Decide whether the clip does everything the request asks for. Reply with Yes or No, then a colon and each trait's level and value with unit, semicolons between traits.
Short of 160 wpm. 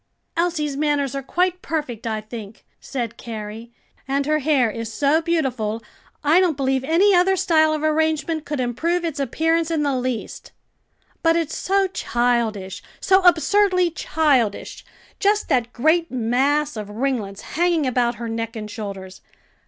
Yes: average, 150 wpm